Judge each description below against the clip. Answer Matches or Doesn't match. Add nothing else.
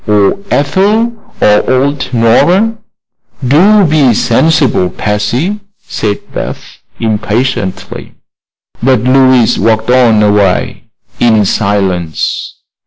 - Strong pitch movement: Matches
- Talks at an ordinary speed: Doesn't match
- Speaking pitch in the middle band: Doesn't match